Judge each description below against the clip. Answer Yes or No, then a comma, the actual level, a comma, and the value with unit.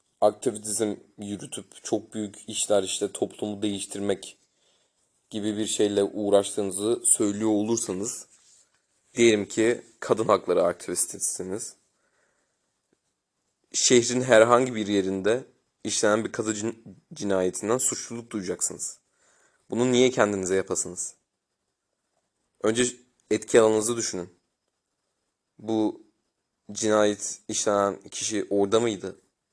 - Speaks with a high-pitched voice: No, low, 105 Hz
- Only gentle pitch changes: Yes, narrow, 2.0 semitones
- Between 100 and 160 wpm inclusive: No, slow, 90 wpm